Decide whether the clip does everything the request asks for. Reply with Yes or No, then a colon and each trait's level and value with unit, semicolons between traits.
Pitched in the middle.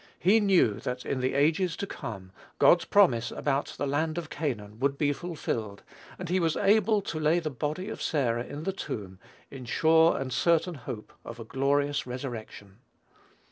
Yes: medium, 145 Hz